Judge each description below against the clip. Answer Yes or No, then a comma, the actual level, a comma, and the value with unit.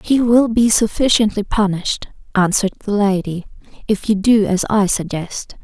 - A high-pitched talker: Yes, high, 205 Hz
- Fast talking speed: No, average, 150 wpm